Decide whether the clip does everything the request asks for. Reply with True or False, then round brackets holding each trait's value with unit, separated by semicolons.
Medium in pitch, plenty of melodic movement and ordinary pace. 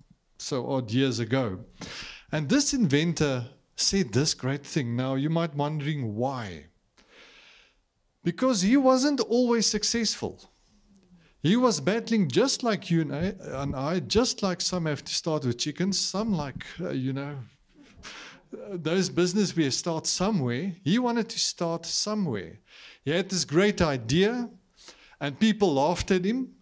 True (175 Hz; 6.6 semitones; 145 wpm)